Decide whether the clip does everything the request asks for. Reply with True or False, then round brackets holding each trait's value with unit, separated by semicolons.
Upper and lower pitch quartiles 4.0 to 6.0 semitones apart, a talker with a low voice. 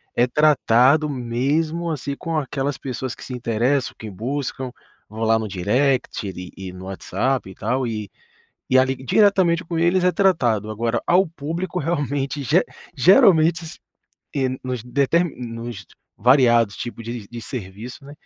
True (5.0 semitones; 130 Hz)